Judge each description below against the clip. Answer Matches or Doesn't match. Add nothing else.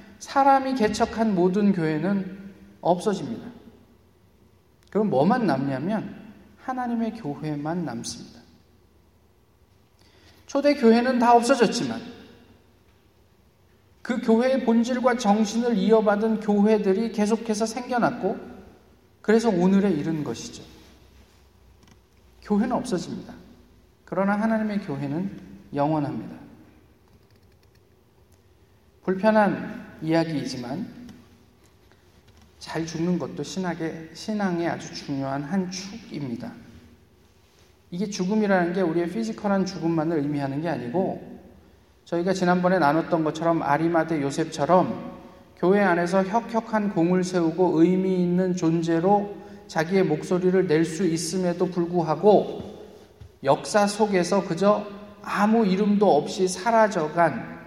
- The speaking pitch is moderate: Matches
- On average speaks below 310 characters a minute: Matches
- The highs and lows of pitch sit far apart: Matches